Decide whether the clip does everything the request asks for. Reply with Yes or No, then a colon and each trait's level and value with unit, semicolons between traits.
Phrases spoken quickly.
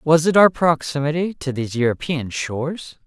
No: average, 155 wpm